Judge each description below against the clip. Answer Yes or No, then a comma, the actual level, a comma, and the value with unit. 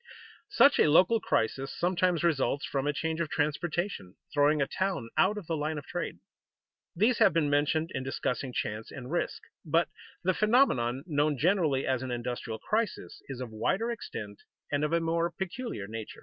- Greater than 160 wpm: Yes, average, 180 wpm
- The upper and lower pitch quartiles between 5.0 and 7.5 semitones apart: Yes, average, 5.3 semitones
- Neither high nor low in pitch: Yes, medium, 150 Hz